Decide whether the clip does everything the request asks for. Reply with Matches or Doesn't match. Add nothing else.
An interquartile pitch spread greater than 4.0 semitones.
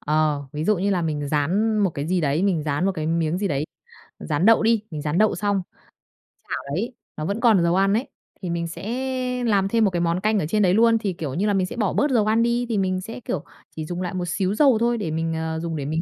Matches